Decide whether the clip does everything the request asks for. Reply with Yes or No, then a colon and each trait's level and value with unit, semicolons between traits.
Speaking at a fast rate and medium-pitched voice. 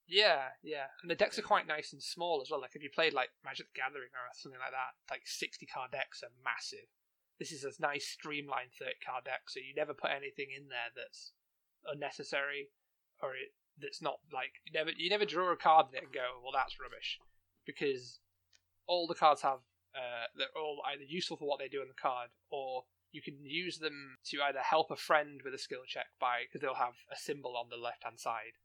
Yes: fast, 220 wpm; medium, 155 Hz